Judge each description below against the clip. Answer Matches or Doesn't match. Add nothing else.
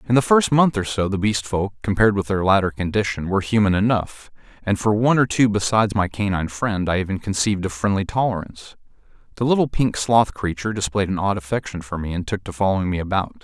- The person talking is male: Matches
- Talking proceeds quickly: Matches